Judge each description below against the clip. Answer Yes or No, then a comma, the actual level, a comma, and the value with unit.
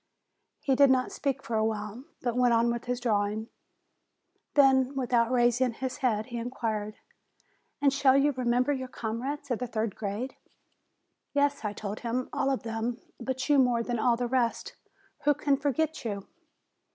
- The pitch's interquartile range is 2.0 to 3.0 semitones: Yes, average, 2.7 semitones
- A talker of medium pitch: No, high, 245 Hz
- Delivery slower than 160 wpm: No, average, 175 wpm